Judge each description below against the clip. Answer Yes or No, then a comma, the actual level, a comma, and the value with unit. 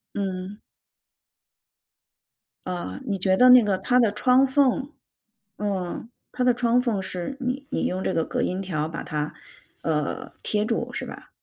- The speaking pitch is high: Yes, high, 205 Hz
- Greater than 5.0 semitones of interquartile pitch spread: Yes, wide, 5.4 semitones